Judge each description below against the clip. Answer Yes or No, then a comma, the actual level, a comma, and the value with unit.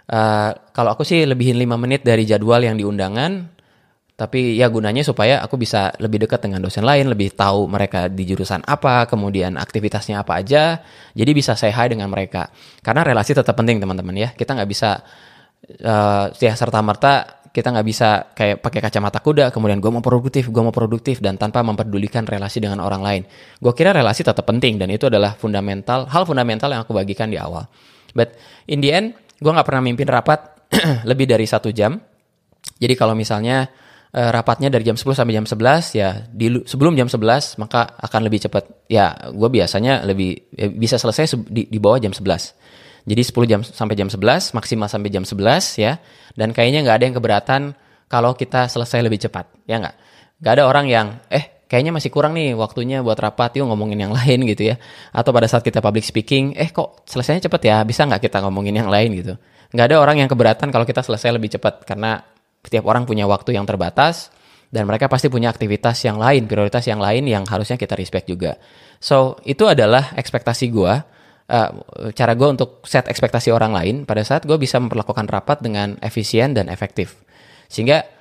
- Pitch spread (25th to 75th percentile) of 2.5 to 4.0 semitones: Yes, average, 3.7 semitones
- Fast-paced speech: Yes, fast, 190 wpm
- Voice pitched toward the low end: Yes, low, 115 Hz